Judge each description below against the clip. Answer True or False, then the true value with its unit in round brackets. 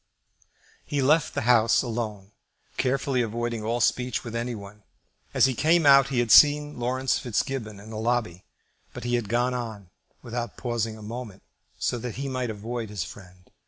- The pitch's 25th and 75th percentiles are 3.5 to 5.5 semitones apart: False (2.7 semitones)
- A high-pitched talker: False (120 Hz)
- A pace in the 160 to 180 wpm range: True (175 wpm)